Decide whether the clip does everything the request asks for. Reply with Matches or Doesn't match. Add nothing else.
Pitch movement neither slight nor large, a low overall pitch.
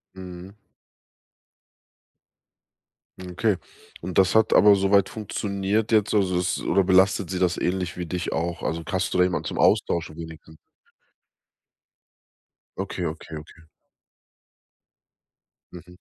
Doesn't match